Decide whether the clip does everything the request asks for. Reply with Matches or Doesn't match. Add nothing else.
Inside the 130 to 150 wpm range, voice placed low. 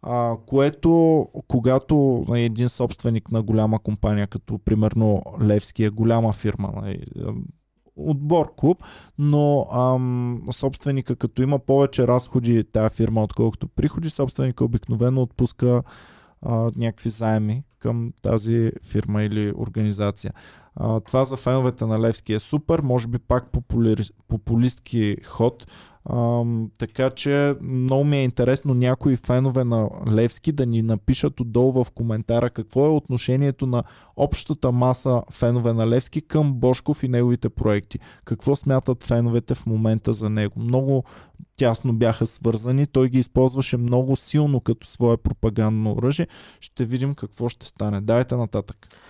Matches